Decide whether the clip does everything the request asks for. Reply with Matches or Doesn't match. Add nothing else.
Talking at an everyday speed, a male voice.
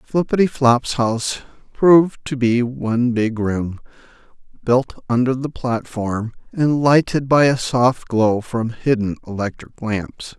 Doesn't match